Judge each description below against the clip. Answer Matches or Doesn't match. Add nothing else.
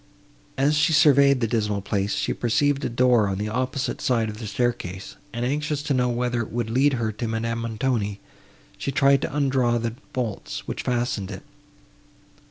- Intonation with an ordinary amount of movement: Matches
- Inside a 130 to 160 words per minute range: Doesn't match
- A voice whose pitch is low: Matches